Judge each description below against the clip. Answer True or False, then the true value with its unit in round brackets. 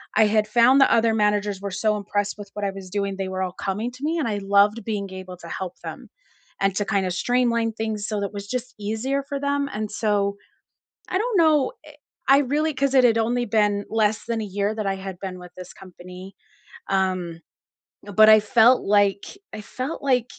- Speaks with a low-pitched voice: False (210 Hz)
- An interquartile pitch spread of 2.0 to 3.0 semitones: False (3.6 semitones)